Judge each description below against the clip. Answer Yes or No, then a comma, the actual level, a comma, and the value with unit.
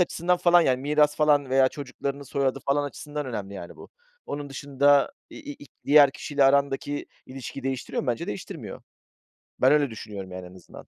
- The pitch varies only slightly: Yes, narrow, 2.2 semitones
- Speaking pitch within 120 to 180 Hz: Yes, medium, 140 Hz